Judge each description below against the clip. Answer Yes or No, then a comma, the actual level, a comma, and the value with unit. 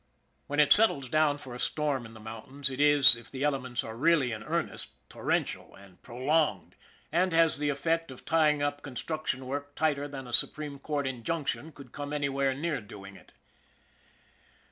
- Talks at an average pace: Yes, average, 180 wpm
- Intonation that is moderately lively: Yes, average, 3.1 semitones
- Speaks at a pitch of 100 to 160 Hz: Yes, medium, 140 Hz